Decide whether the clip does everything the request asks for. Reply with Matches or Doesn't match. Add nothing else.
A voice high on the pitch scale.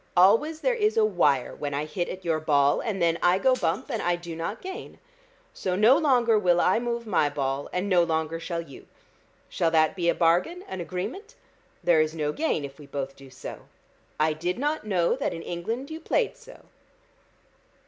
Doesn't match